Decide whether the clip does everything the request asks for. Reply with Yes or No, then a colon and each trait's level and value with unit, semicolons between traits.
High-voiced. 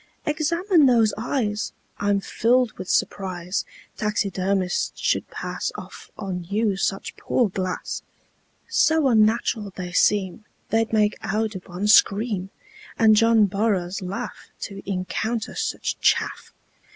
Yes: high, 210 Hz